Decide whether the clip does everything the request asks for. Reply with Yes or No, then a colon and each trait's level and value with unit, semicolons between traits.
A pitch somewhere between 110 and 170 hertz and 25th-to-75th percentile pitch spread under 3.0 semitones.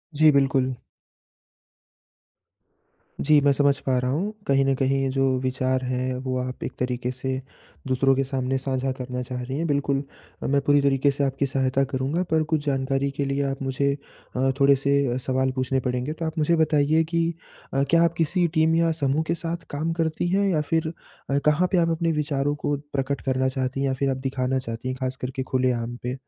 Yes: low, 135 Hz; narrow, 2.6 semitones